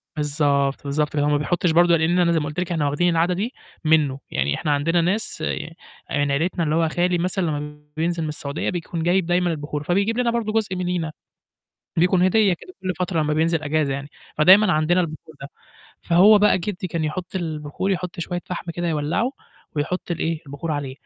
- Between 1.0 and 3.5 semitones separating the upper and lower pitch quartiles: Yes, average, 3.2 semitones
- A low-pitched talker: No, medium, 165 Hz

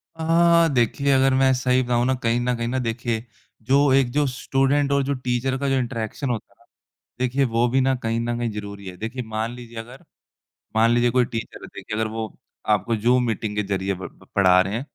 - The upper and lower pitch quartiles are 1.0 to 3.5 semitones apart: Yes, average, 2.8 semitones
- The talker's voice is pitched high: No, low, 120 Hz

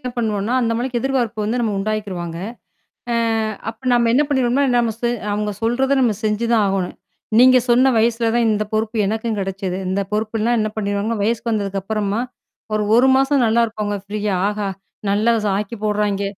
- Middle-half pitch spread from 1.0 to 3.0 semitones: Yes, narrow, 2.5 semitones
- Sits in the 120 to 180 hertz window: No, high, 220 Hz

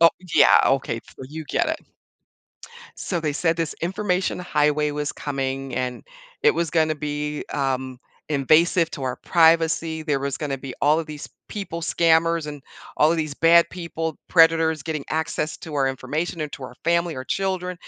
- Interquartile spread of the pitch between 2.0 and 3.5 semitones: Yes, average, 2.7 semitones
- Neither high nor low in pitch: Yes, medium, 155 Hz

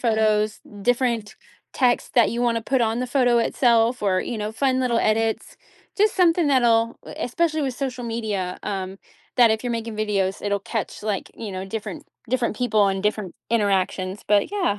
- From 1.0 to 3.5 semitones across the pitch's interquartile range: Yes, average, 2.9 semitones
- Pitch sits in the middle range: No, high, 225 Hz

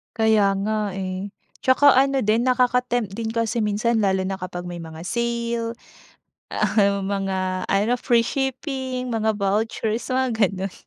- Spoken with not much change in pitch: No, average, 3.7 semitones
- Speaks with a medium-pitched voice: No, high, 220 Hz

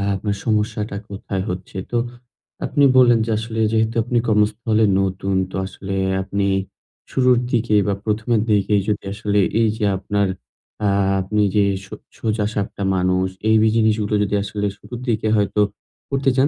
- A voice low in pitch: Yes, low, 105 Hz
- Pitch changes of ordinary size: No, narrow, 1.9 semitones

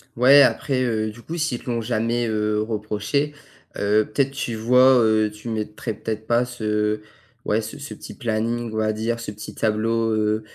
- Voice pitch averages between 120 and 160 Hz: No, low, 110 Hz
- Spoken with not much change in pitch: Yes, narrow, 2.2 semitones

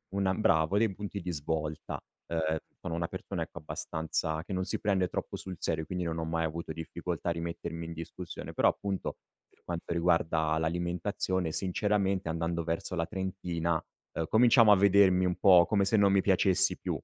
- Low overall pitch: Yes, very low, 85 Hz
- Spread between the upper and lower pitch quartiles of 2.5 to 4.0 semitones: Yes, average, 2.8 semitones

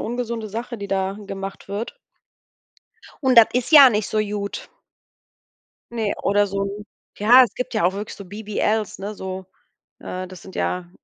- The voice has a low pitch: No, high, 205 Hz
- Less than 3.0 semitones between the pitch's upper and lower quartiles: Yes, narrow, 2.6 semitones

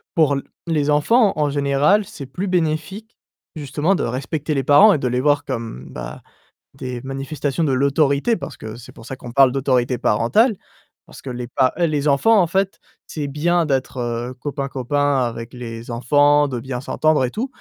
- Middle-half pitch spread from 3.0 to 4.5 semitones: Yes, average, 3.6 semitones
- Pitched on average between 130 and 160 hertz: Yes, medium, 140 Hz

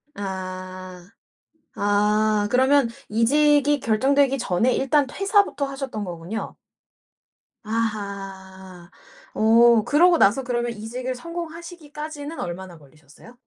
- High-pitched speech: Yes, high, 230 Hz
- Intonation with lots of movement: Yes, wide, 6.6 semitones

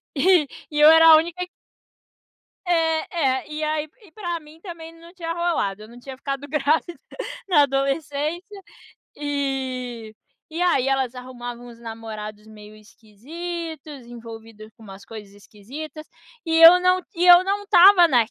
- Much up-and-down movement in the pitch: Yes, wide, 5.8 semitones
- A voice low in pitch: No, very high, 290 Hz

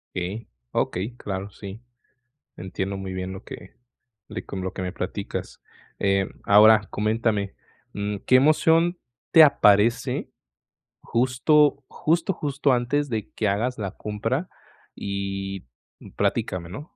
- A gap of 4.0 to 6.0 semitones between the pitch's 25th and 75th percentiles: Yes, average, 4.8 semitones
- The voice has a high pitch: No, low, 105 Hz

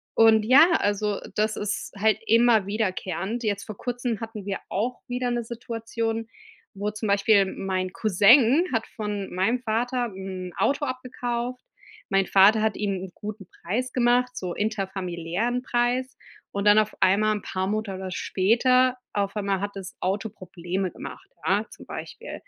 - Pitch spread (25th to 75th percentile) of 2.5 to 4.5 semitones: Yes, average, 3.7 semitones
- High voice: Yes, high, 215 Hz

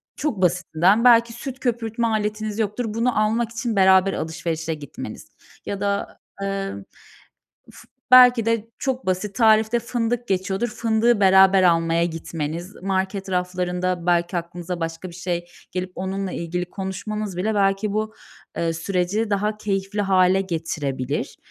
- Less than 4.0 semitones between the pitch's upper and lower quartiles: Yes, average, 3.5 semitones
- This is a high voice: Yes, high, 195 Hz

